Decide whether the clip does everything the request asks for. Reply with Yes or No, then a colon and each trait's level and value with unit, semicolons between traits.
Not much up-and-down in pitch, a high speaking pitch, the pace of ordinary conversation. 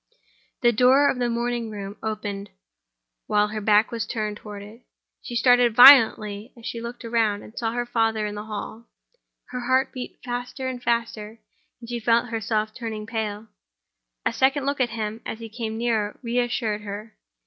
Yes: narrow, 2.3 semitones; high, 230 Hz; average, 180 wpm